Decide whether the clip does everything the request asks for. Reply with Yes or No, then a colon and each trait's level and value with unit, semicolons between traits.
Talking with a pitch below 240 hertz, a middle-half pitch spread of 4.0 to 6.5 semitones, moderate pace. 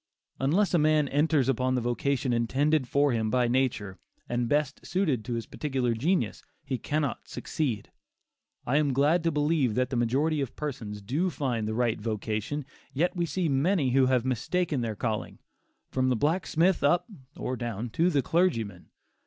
Yes: low, 135 Hz; average, 4.4 semitones; average, 170 wpm